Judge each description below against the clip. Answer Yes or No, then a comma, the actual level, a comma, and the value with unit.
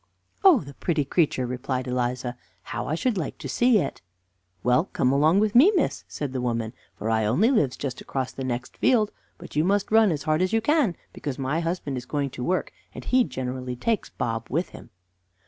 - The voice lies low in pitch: No, medium, 145 Hz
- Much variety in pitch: Yes, wide, 7.6 semitones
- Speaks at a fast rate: Yes, fast, 210 wpm